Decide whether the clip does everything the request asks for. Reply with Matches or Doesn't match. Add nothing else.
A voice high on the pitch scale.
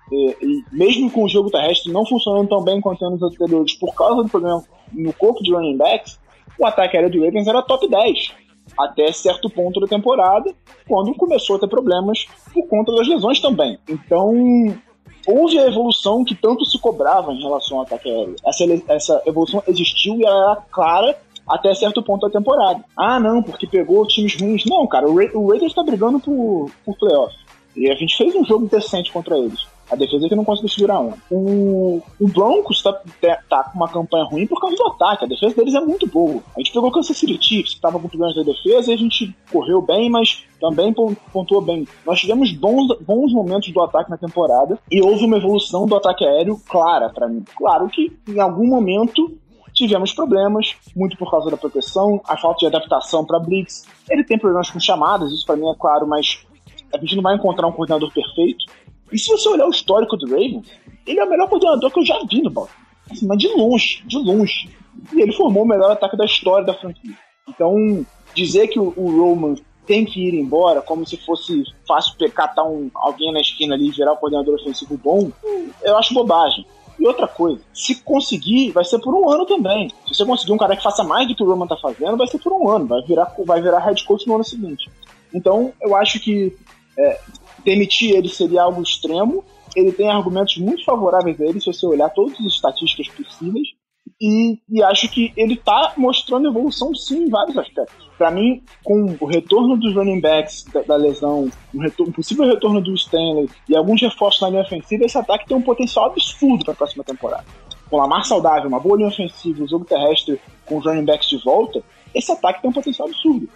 Matches